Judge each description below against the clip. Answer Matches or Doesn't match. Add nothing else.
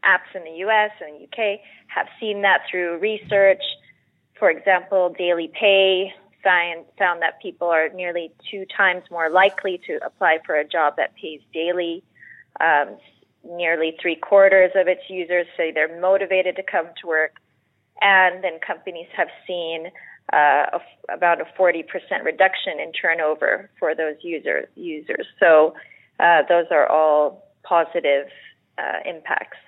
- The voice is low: Doesn't match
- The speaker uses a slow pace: Doesn't match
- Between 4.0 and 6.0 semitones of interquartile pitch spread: Doesn't match